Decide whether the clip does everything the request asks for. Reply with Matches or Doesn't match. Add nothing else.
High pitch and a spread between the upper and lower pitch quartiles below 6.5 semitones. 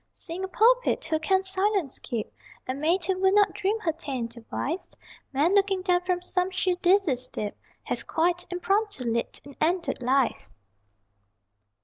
Matches